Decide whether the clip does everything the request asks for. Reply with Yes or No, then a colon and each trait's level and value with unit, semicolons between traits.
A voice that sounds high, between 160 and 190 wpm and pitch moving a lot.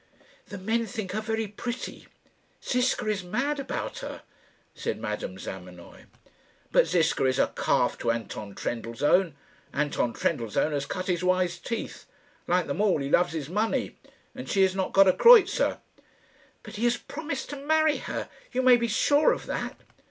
Yes: high, 200 Hz; average, 165 wpm; wide, 6.9 semitones